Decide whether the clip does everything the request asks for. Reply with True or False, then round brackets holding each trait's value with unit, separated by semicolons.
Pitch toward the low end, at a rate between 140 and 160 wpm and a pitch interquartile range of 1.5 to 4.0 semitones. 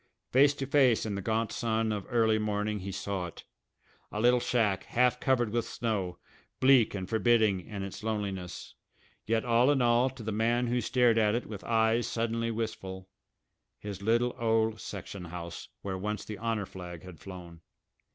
False (110 Hz; 175 wpm; 3.0 semitones)